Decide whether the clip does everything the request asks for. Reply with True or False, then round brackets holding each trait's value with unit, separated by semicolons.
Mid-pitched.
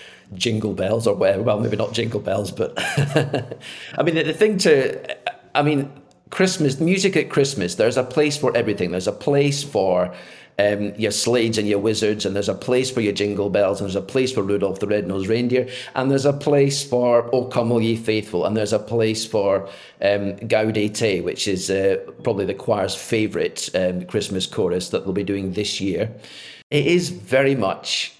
False (115 Hz)